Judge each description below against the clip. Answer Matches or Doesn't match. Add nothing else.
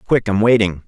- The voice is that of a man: Matches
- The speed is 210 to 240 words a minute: Doesn't match